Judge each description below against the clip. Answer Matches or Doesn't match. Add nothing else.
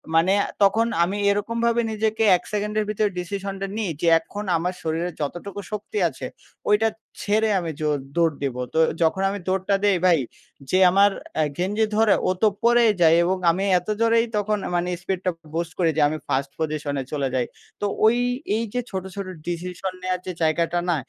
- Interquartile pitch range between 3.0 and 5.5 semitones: Matches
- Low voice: Doesn't match